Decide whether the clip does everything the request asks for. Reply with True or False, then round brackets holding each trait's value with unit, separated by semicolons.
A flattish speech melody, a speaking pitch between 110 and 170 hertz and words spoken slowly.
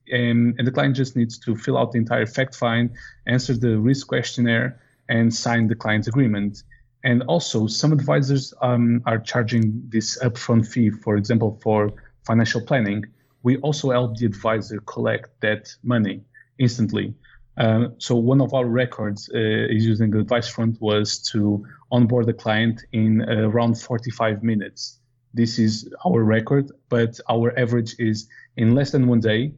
False (2.0 semitones; 115 Hz; 165 wpm)